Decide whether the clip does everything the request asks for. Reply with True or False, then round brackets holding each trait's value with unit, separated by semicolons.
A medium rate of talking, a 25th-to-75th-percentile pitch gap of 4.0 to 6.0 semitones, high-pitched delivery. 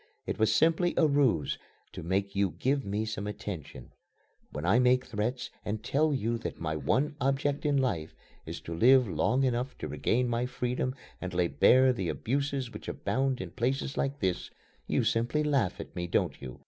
False (185 wpm; 5.5 semitones; 120 Hz)